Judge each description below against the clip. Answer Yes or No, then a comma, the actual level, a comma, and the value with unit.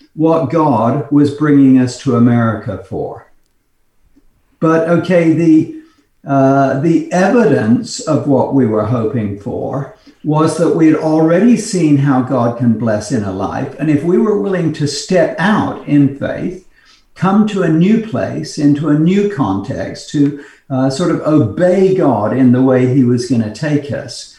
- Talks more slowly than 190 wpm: Yes, average, 165 wpm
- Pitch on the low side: No, medium, 145 Hz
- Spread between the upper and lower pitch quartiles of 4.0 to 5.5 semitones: Yes, average, 4.3 semitones